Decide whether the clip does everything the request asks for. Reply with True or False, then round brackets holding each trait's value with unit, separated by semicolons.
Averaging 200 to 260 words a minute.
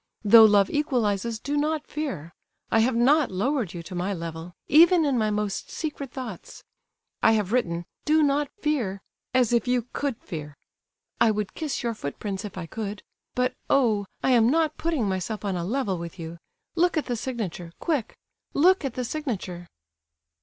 False (170 wpm)